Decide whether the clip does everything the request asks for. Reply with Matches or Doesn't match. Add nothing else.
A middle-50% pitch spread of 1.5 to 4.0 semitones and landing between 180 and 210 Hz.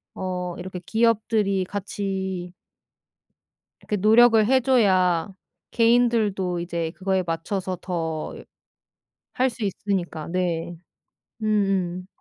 Matches